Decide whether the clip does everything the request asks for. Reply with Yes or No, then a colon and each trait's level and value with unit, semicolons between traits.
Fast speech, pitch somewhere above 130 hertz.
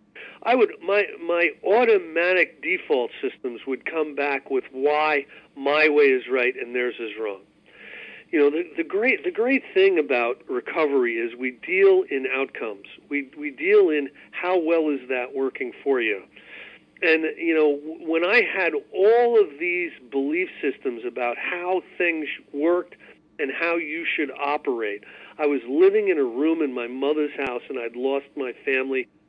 No: average, 165 wpm; medium, 185 Hz